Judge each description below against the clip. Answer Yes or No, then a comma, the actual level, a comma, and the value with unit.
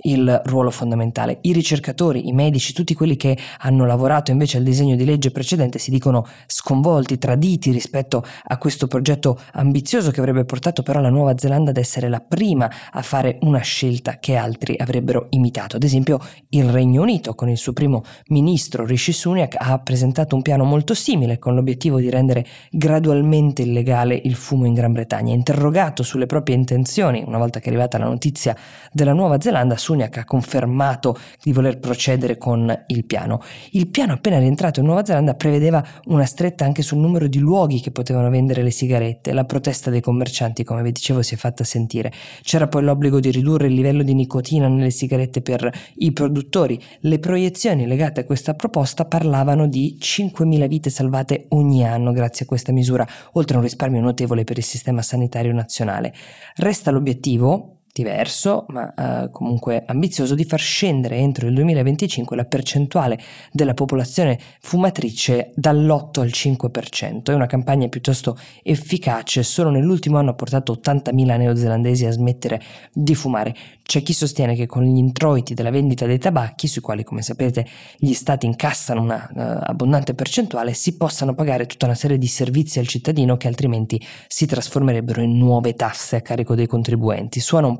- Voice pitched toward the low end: Yes, low, 130 Hz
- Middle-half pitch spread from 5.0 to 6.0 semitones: No, average, 3.1 semitones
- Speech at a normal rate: No, fast, 175 wpm